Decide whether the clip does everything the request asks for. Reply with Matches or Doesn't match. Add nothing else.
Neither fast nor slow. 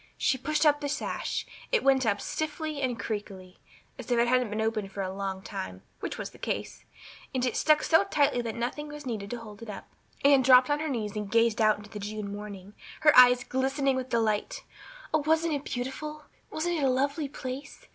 Doesn't match